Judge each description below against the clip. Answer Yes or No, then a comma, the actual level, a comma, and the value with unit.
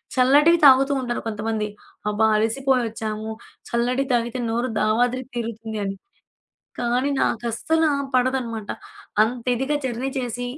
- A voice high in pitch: Yes, high, 240 Hz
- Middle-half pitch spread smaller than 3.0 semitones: Yes, narrow, 2.6 semitones